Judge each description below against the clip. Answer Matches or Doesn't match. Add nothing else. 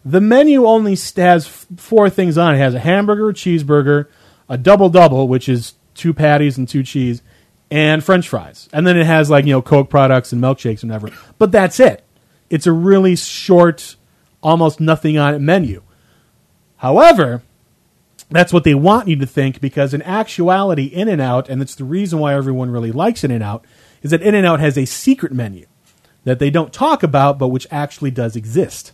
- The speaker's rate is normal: Matches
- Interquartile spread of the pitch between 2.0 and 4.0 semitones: Doesn't match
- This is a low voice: Doesn't match